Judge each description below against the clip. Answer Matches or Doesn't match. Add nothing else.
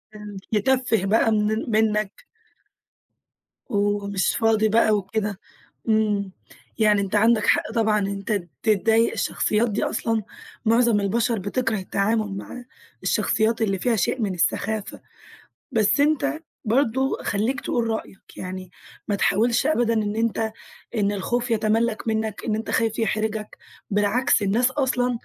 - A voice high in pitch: Matches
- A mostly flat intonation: Matches